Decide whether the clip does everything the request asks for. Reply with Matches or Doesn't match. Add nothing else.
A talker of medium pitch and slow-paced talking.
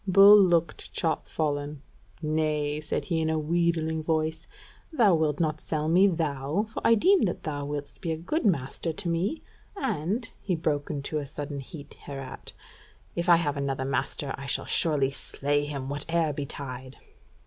Doesn't match